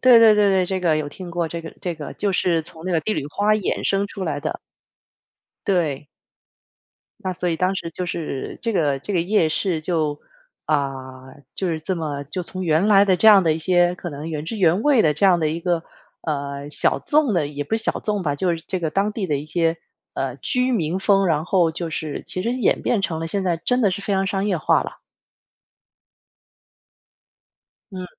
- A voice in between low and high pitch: Yes, medium, 175 Hz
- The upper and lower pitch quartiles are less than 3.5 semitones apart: No, average, 3.8 semitones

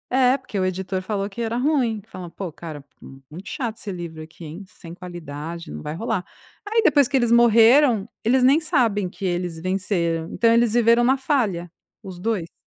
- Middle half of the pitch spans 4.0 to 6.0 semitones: Yes, wide, 5.4 semitones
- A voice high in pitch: Yes, high, 200 Hz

